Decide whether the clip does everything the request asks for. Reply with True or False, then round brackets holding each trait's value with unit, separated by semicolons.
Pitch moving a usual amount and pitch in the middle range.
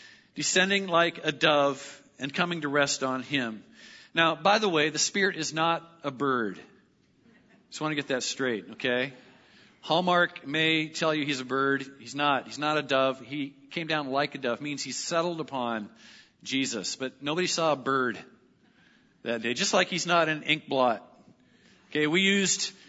True (3.8 semitones; 145 Hz)